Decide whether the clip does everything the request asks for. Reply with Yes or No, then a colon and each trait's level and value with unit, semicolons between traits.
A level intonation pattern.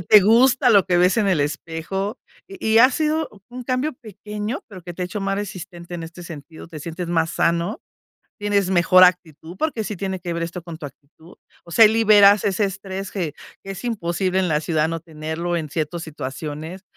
No: average, 3.8 semitones